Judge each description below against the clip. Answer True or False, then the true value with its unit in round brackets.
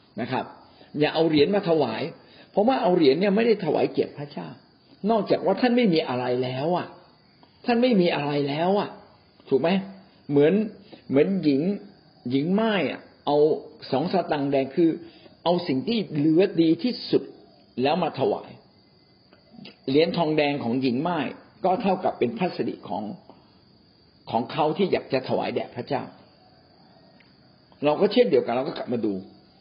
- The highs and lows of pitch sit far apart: True (5.7 semitones)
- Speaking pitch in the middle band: True (155 Hz)